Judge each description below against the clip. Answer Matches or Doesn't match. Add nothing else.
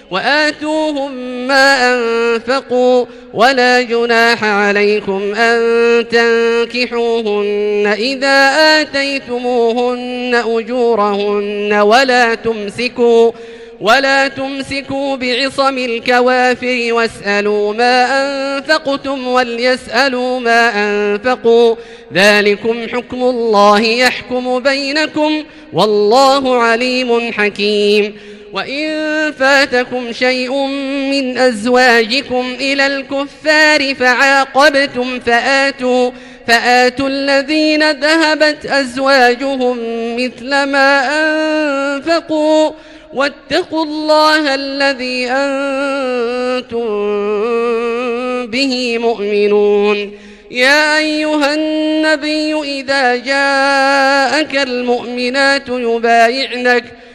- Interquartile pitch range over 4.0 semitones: Doesn't match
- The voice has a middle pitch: Doesn't match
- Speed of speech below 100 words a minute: Matches